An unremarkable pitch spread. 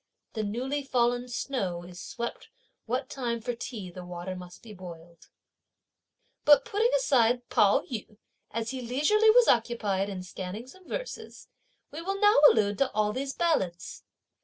No: wide, 5.9 semitones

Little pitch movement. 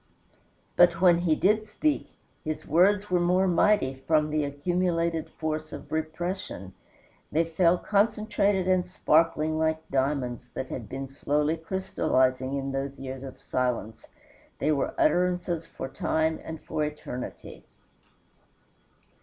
No: average, 4.3 semitones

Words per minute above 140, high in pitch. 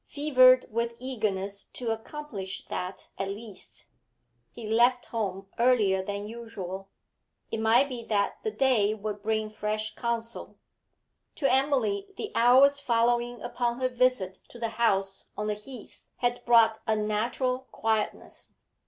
No: slow, 135 wpm; high, 230 Hz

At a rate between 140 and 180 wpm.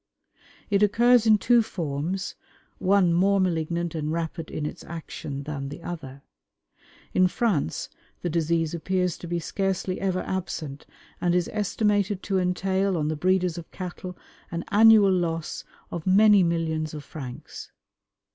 Yes: average, 145 wpm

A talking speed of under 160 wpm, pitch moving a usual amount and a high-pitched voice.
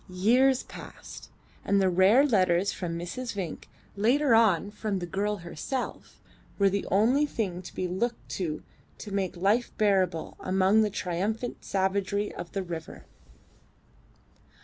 Yes: average, 140 wpm; average, 3.2 semitones; high, 200 Hz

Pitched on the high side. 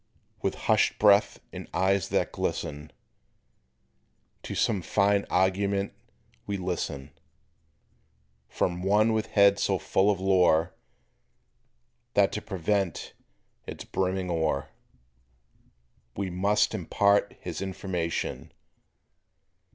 No: very low, 95 Hz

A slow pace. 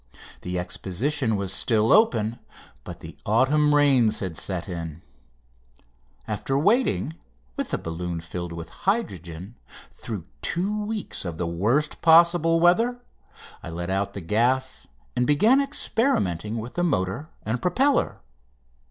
Yes: slow, 130 wpm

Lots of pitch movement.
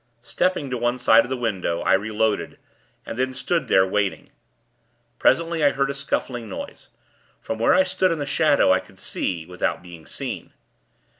Yes: wide, 6.4 semitones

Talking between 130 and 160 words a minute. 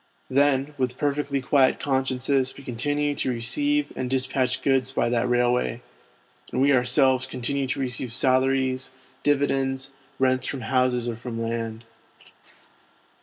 Yes: slow, 135 wpm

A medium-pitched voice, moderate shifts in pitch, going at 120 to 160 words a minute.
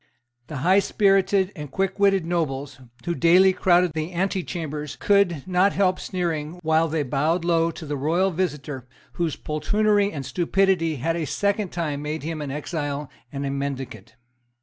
Yes: medium, 165 Hz; average, 3.9 semitones; average, 150 wpm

